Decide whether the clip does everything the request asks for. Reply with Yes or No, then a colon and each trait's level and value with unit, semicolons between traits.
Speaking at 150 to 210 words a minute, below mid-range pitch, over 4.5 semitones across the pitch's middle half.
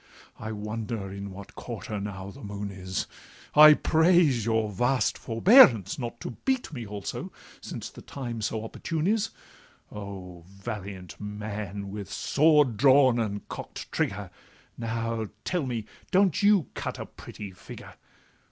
No: average, 140 wpm; low, 110 Hz; average, 5.1 semitones